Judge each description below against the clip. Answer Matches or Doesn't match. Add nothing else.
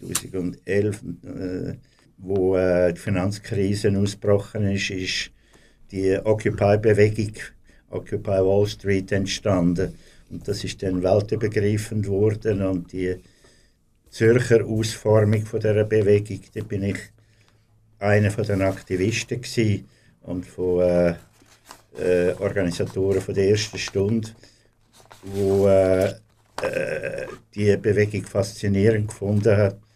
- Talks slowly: Matches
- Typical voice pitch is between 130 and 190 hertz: Doesn't match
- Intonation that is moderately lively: Doesn't match